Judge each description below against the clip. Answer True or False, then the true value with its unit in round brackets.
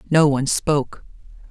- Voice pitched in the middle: True (145 Hz)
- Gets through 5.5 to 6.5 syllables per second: True (5.8 syllables/s)